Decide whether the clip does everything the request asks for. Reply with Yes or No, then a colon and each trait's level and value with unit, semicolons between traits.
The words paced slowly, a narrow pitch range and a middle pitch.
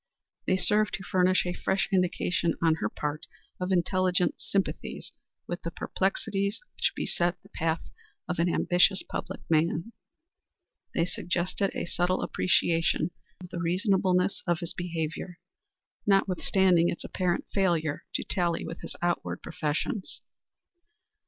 Yes: slow, 130 wpm; narrow, 2.0 semitones; medium, 180 Hz